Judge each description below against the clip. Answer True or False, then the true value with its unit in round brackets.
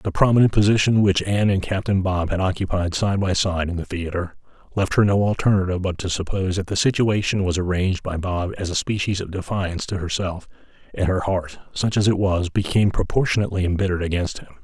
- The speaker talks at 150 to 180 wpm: False (200 wpm)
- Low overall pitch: True (95 Hz)